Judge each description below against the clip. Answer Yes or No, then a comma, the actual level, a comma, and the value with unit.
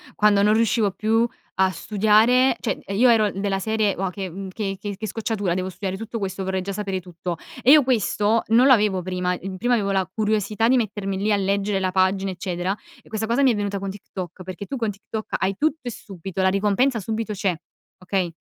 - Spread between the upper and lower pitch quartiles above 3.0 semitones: No, narrow, 2.6 semitones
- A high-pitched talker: Yes, high, 200 Hz